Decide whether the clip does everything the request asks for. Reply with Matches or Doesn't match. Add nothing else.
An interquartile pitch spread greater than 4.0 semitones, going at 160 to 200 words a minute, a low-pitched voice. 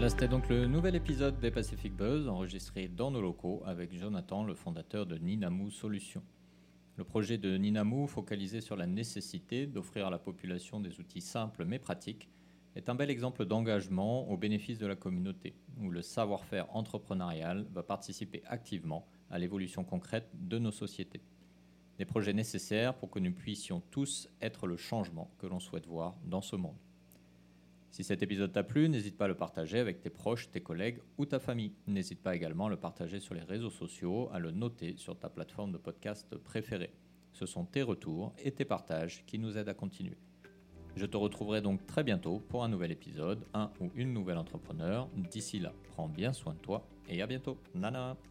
Matches